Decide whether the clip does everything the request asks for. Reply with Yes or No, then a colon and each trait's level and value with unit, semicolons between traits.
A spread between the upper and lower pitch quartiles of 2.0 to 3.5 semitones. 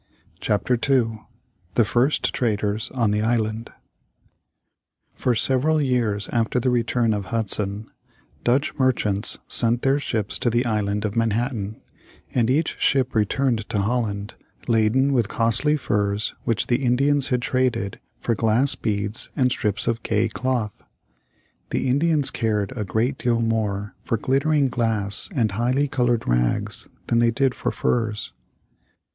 Yes: average, 3.2 semitones